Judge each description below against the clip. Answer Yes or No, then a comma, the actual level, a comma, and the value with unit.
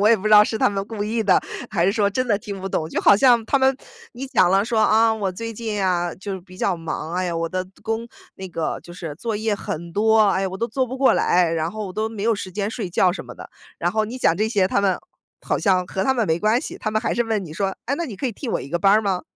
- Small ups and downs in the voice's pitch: No, average, 3.3 semitones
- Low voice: No, high, 205 Hz